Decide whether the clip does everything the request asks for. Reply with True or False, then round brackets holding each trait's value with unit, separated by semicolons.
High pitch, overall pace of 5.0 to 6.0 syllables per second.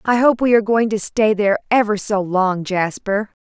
True (210 Hz; 5.1 syllables/s)